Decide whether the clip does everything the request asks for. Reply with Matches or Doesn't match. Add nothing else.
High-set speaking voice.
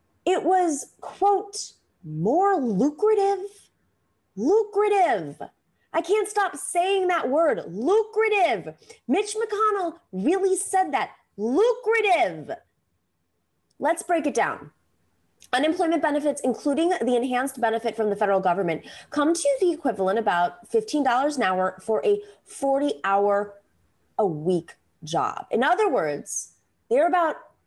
Matches